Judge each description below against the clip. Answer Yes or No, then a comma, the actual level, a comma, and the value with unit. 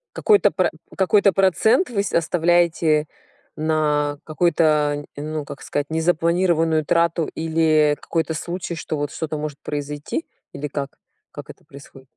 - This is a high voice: No, medium, 160 Hz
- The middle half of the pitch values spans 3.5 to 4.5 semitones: No, narrow, 2.5 semitones